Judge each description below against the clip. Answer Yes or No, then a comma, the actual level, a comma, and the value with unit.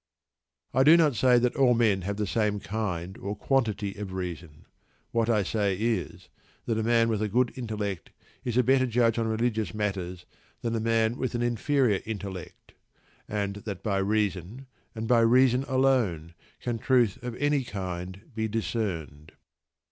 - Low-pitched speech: Yes, low, 110 Hz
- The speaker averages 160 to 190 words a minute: Yes, average, 165 wpm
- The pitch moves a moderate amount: Yes, average, 3.5 semitones